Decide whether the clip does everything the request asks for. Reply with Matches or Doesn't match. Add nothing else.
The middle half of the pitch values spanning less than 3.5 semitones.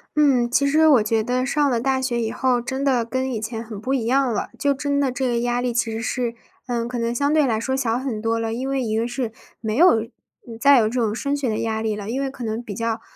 Matches